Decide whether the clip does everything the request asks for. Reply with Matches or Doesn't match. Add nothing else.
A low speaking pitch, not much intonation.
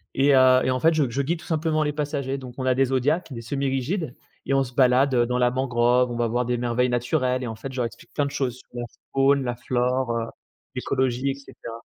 Matches